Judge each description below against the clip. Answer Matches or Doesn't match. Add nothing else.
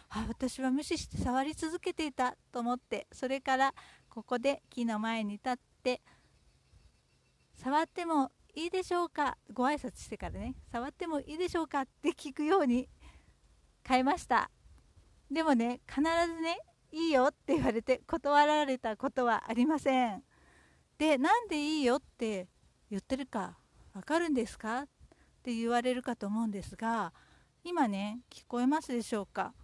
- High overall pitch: Matches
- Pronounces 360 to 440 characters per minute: Doesn't match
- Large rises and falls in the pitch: Doesn't match